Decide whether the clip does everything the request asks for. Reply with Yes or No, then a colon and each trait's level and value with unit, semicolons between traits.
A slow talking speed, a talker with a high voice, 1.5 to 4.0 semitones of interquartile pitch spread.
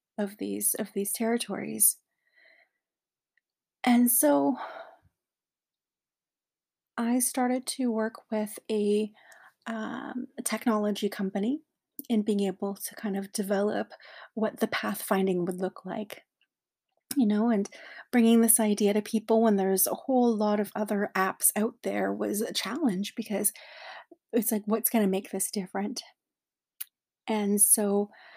Yes: slow, 130 wpm; high, 215 Hz; average, 2.7 semitones